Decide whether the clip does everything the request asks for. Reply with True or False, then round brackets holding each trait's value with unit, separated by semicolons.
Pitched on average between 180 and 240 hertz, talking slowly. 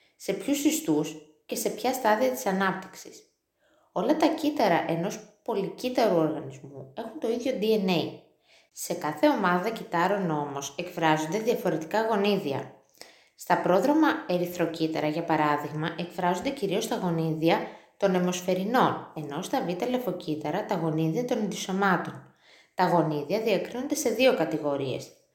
False (185 Hz; 125 wpm)